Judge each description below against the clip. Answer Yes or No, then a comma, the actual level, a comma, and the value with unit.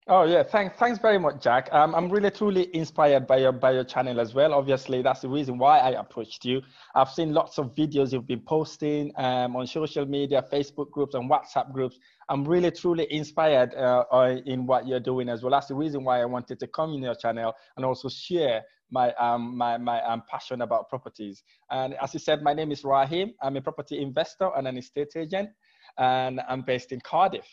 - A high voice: No, low, 135 Hz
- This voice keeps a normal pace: No, fast, 215 wpm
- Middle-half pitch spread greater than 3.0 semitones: Yes, average, 3.4 semitones